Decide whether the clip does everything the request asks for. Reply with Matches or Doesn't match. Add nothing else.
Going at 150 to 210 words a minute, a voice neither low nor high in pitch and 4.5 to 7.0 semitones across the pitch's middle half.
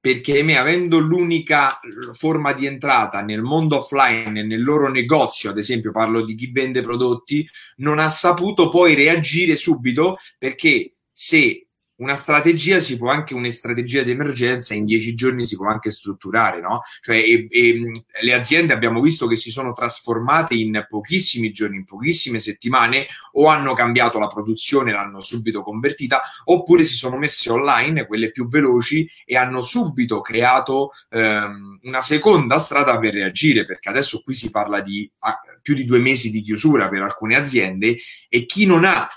Doesn't match